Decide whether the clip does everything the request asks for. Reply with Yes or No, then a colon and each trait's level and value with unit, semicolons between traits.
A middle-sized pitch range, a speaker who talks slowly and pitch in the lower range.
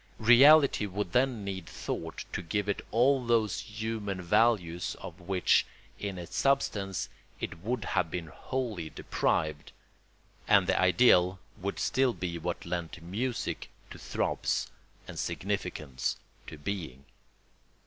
Yes: average, 4.7 semitones; slow, 130 wpm; low, 100 Hz